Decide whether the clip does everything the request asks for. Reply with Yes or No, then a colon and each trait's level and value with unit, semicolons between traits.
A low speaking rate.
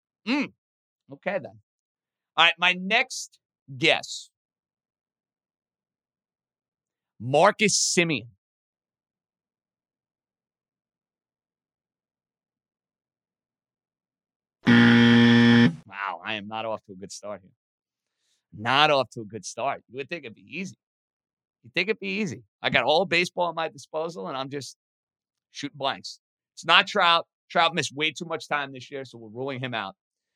Yes: slow, 130 wpm